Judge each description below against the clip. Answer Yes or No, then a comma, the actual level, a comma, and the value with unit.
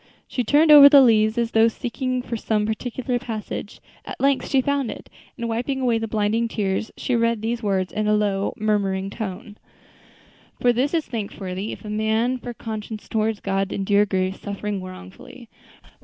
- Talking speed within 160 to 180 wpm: Yes, average, 175 wpm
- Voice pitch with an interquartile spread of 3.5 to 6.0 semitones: No, average, 2.9 semitones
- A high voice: Yes, high, 220 Hz